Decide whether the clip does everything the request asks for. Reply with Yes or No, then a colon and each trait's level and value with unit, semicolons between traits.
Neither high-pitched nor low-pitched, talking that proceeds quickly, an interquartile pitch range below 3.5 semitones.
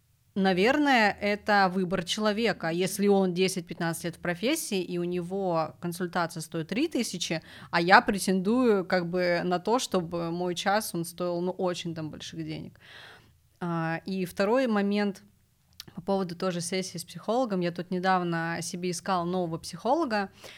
No: medium, 180 Hz; average, 145 wpm; narrow, 2.6 semitones